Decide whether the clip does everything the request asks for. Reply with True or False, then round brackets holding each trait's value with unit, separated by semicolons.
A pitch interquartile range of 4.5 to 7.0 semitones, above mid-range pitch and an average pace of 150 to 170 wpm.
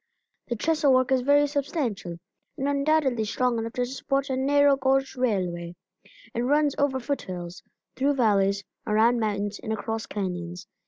True (5.1 semitones; 250 Hz; 155 wpm)